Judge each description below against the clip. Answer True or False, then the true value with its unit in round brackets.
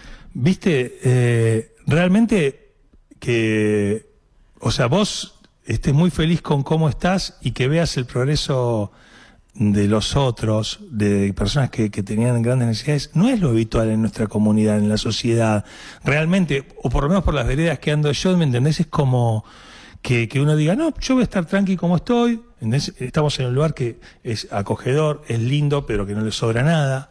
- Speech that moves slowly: False (180 wpm)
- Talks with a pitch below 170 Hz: True (135 Hz)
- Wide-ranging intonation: True (6.2 semitones)